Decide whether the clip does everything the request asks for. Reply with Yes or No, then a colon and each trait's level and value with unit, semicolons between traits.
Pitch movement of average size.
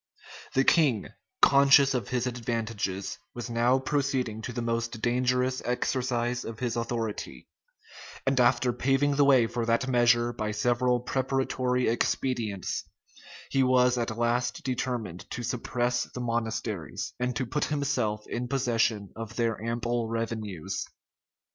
No: narrow, 1.9 semitones